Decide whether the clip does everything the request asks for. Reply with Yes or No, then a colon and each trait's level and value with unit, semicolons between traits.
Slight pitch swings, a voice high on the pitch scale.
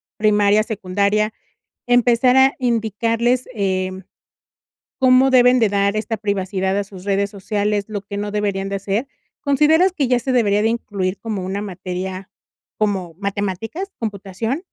No: average, 3.2 semitones; high, 210 Hz